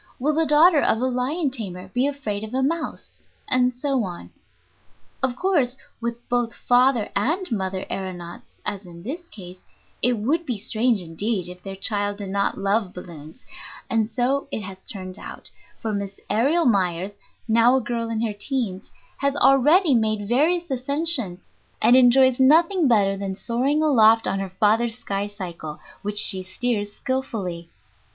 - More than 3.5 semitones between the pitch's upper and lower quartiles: Yes, average, 5.1 semitones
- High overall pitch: Yes, high, 230 Hz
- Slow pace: No, average, 160 wpm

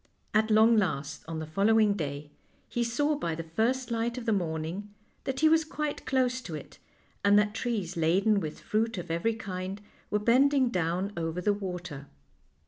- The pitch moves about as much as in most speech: No, wide, 5.7 semitones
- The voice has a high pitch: Yes, high, 205 Hz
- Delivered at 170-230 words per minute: Yes, average, 180 wpm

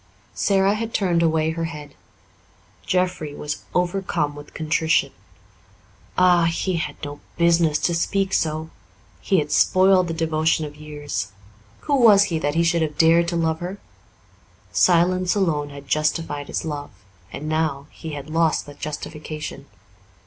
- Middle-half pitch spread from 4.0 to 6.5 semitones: No, average, 3.0 semitones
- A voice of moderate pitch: Yes, medium, 160 Hz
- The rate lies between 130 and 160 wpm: Yes, average, 150 wpm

